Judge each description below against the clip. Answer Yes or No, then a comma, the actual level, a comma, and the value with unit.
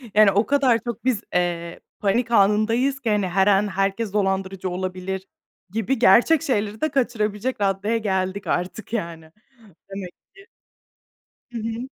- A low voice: No, high, 205 Hz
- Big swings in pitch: No, average, 3.4 semitones